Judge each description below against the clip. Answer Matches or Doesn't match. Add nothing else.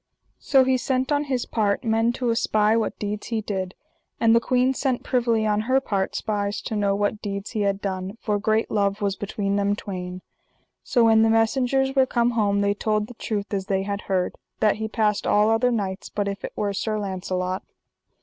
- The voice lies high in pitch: Matches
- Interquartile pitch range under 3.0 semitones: Matches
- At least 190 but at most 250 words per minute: Matches